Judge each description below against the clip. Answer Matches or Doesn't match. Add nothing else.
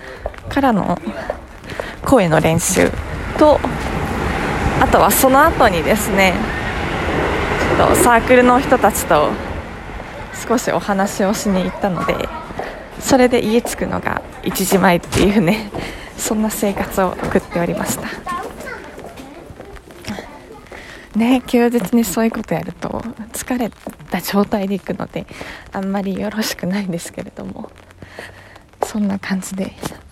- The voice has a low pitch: Doesn't match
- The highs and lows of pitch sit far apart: Doesn't match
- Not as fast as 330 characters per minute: Matches